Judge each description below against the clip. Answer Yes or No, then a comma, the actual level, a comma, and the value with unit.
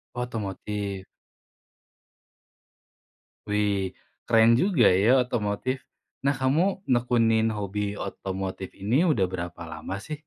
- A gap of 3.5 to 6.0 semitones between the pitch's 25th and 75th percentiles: Yes, average, 4.1 semitones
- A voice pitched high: No, low, 110 Hz